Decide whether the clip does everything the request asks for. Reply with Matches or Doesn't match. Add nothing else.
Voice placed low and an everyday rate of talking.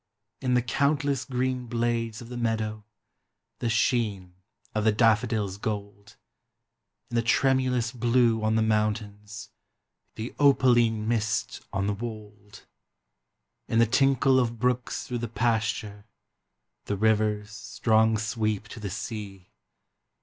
Doesn't match